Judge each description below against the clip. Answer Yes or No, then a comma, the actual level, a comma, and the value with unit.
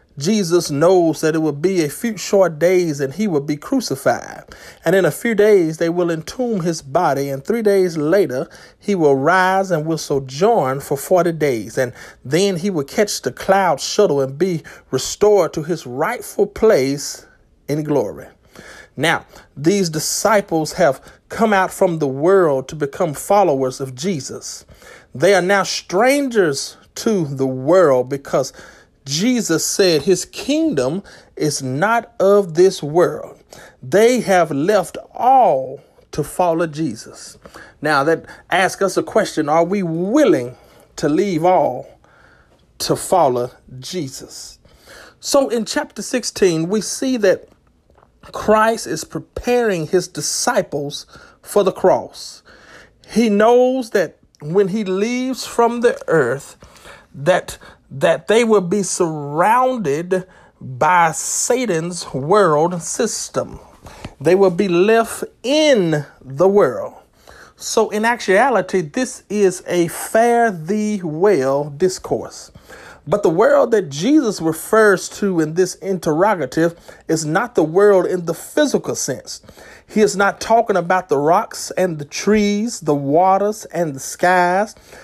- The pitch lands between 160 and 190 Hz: Yes, medium, 185 Hz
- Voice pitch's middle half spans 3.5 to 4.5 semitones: No, average, 5.1 semitones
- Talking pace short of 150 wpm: Yes, slow, 135 wpm